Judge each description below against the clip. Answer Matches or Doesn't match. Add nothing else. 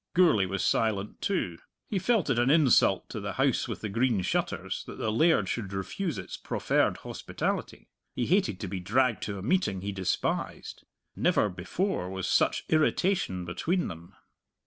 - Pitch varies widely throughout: Matches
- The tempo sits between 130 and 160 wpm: Doesn't match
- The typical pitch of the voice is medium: Doesn't match